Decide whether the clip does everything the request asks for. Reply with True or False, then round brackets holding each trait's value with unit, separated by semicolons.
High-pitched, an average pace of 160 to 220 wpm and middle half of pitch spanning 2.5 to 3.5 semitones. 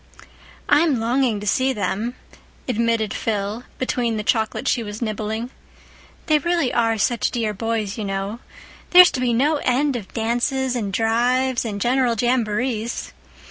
False (235 Hz; 145 wpm; 3.0 semitones)